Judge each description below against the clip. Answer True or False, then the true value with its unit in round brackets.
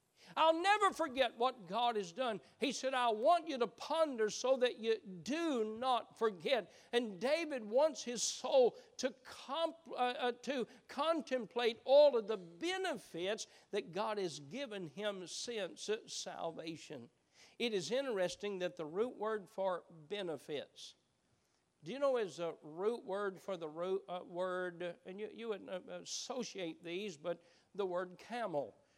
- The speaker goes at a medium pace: True (150 wpm)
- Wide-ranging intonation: True (6.0 semitones)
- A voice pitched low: False (225 Hz)